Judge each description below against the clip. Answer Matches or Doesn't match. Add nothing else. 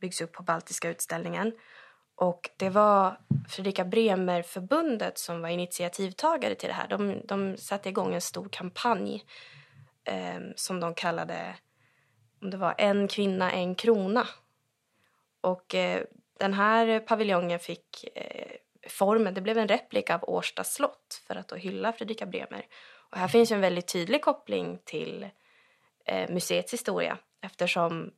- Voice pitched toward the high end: Matches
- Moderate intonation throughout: Matches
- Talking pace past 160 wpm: Doesn't match